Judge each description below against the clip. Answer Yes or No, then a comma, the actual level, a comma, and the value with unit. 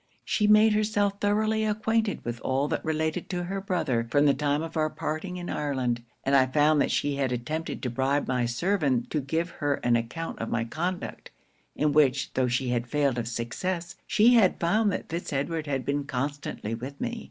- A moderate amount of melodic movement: No, wide, 5.7 semitones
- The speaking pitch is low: No, medium, 150 Hz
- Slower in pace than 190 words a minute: No, average, 200 wpm